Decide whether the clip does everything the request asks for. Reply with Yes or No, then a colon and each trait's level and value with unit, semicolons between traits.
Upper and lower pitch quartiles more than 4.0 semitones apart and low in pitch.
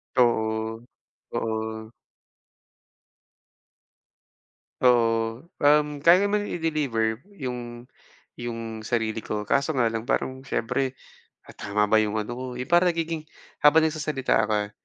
Yes: average, 5.0 semitones; low, 120 Hz